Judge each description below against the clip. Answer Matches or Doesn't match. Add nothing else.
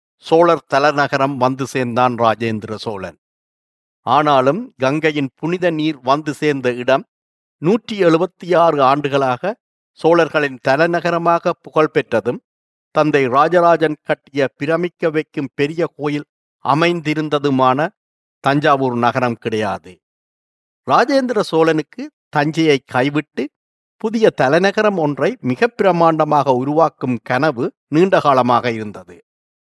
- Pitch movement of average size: Matches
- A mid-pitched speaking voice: Matches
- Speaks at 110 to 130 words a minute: Doesn't match